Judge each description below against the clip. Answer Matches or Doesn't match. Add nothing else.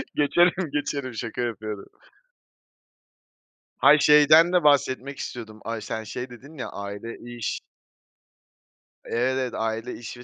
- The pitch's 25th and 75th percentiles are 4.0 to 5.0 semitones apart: Matches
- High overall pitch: Doesn't match